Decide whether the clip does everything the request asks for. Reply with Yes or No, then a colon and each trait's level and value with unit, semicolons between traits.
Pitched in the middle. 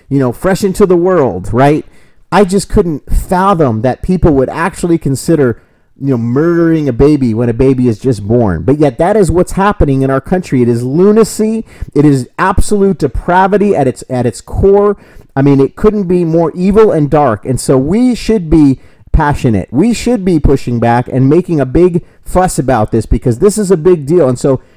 Yes: medium, 150 Hz